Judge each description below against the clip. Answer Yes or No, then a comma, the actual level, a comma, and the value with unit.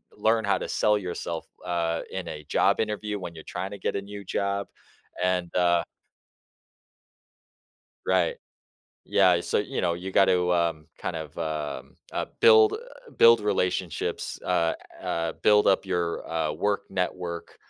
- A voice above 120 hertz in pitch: No, very low, 90 Hz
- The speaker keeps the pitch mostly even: No, average, 3.1 semitones